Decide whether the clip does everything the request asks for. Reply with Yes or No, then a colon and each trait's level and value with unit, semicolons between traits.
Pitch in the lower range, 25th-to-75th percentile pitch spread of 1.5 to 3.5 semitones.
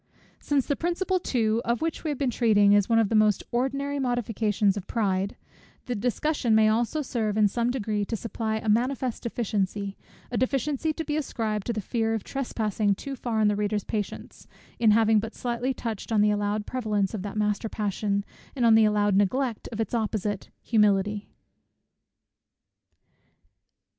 No: high, 220 Hz; average, 2.9 semitones